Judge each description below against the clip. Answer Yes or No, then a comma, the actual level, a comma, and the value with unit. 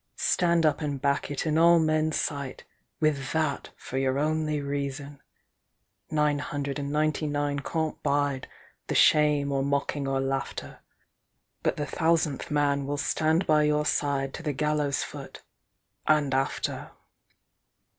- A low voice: No, medium, 145 Hz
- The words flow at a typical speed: No, slow, 125 wpm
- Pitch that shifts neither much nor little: No, narrow, 1.6 semitones